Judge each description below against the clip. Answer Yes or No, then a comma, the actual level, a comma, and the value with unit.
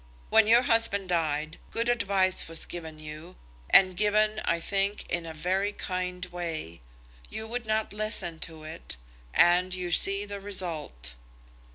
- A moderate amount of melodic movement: Yes, average, 3.9 semitones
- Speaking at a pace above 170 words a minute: No, average, 150 wpm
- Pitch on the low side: No, medium, 185 Hz